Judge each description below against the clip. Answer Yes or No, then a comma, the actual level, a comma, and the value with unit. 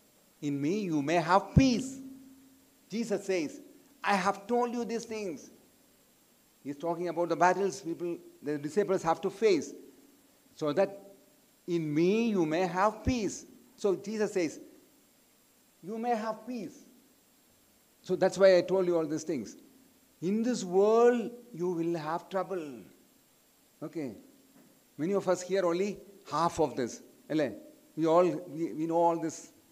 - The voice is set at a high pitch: Yes, high, 200 Hz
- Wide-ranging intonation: Yes, wide, 7.3 semitones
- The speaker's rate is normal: No, fast, 145 wpm